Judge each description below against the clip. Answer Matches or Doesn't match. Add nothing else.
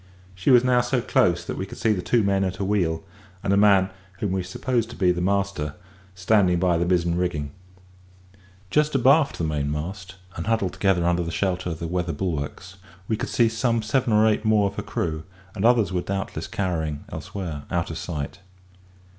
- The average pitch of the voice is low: Matches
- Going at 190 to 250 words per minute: Matches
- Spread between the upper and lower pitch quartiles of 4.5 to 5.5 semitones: Doesn't match